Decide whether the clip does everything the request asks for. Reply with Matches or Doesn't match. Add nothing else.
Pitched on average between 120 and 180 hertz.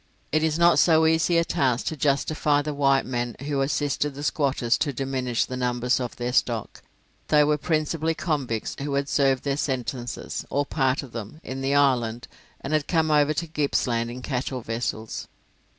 Matches